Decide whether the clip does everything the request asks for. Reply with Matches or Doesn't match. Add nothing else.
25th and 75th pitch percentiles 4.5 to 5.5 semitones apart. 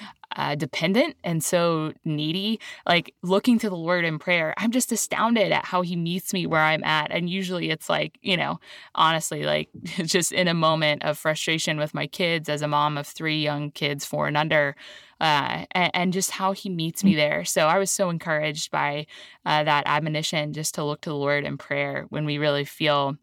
Doesn't match